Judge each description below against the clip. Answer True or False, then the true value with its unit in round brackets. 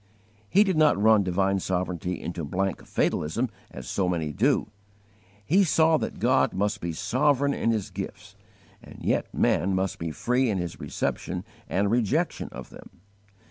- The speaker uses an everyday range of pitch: False (5.9 semitones)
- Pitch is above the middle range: False (100 Hz)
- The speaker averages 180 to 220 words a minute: False (160 wpm)